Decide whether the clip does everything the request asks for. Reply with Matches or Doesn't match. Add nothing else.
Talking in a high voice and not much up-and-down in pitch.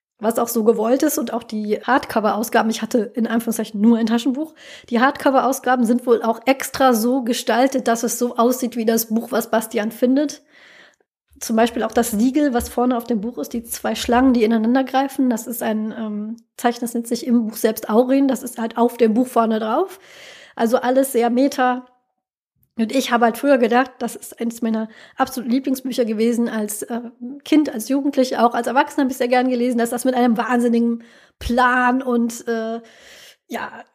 Matches